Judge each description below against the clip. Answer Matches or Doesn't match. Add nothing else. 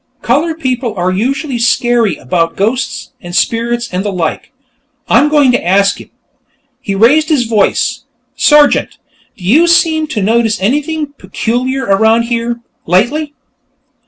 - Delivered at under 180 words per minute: Matches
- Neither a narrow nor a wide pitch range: Doesn't match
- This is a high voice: Matches